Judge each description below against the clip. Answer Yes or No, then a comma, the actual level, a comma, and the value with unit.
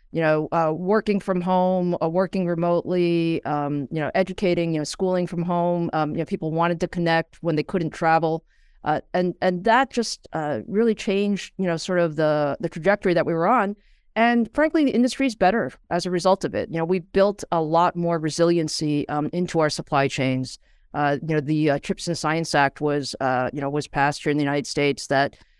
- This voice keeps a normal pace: No, fast, 220 wpm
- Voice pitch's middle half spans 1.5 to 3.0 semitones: No, average, 3.4 semitones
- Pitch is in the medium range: Yes, medium, 170 Hz